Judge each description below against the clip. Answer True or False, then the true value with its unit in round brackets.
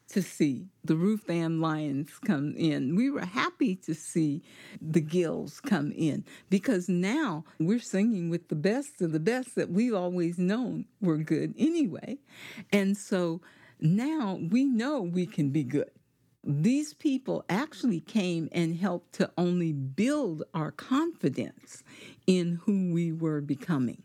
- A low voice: False (180 Hz)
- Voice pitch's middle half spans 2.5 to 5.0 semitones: False (5.6 semitones)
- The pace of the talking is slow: False (145 wpm)